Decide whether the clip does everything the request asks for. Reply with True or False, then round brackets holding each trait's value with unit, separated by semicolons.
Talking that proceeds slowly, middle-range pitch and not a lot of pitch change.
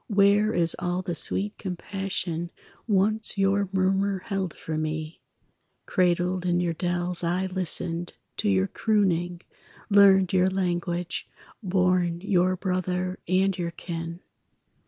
True (120 wpm; 180 Hz; 1.8 semitones)